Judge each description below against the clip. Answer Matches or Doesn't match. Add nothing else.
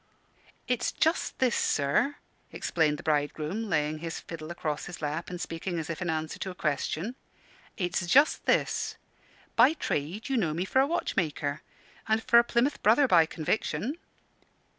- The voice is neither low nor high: Matches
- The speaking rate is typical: Matches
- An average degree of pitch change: Doesn't match